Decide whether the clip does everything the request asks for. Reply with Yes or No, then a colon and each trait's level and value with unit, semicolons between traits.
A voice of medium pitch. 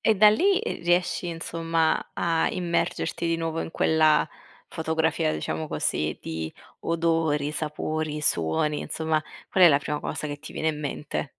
Yes: medium, 160 Hz